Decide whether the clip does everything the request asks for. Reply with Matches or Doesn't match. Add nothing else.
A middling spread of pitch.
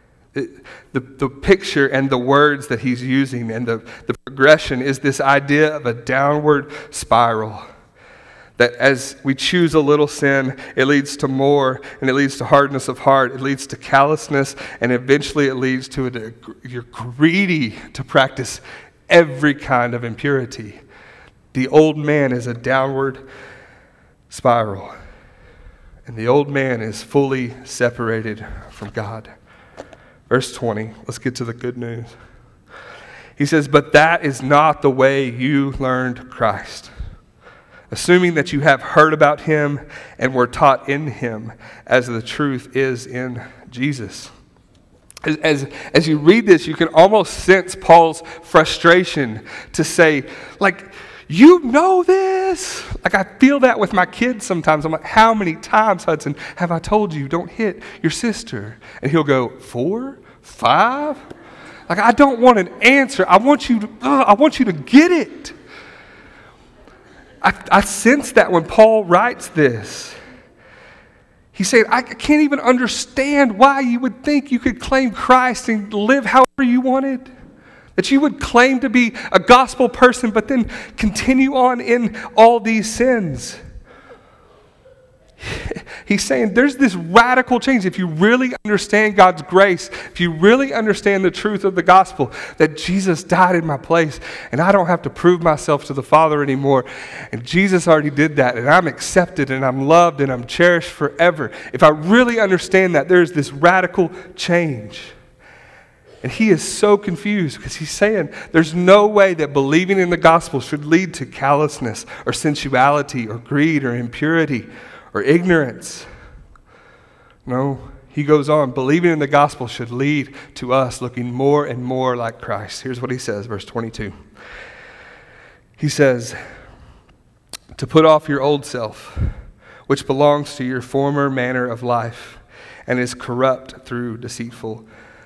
Doesn't match